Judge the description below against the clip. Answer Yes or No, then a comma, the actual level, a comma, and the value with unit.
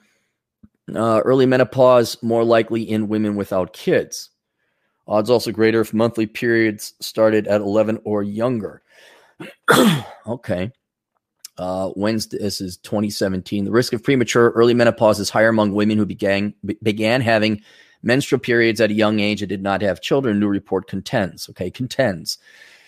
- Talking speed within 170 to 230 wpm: No, average, 150 wpm